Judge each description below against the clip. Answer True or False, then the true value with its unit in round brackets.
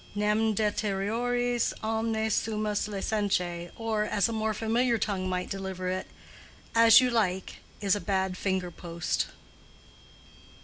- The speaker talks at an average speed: False (125 wpm)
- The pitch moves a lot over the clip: False (2.8 semitones)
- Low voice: False (210 Hz)